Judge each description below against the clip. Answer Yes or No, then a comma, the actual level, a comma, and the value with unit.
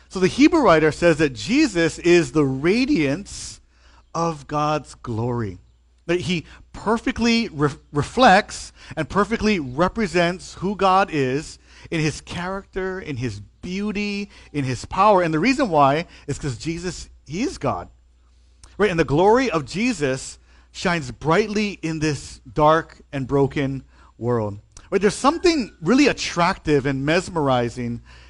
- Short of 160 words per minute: Yes, slow, 135 wpm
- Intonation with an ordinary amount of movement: No, wide, 6.6 semitones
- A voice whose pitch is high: No, medium, 160 Hz